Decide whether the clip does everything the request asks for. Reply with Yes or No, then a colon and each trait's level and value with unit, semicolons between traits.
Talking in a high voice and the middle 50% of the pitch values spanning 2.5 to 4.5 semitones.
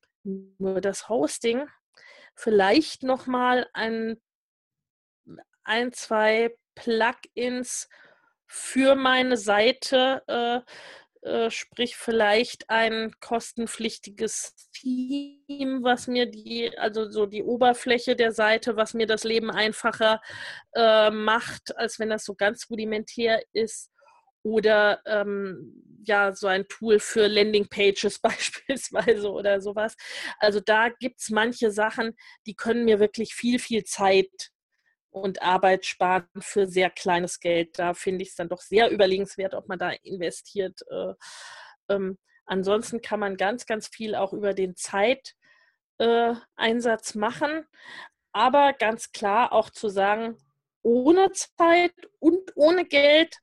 Yes: high, 225 Hz; average, 3.4 semitones